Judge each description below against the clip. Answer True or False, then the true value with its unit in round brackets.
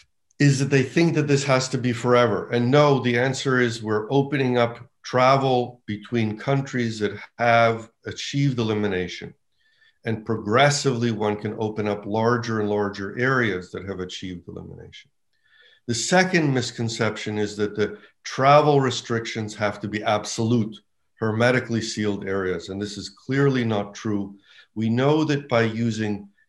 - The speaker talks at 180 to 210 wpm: False (145 wpm)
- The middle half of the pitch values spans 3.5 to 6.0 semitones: True (3.9 semitones)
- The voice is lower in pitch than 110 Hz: False (115 Hz)